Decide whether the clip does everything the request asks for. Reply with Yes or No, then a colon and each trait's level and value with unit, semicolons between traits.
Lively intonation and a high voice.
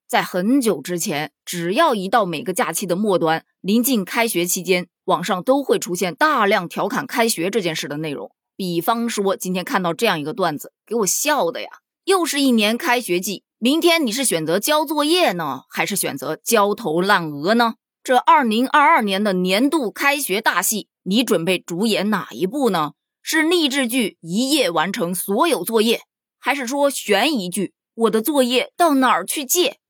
Yes: wide, 6.3 semitones; high, 215 Hz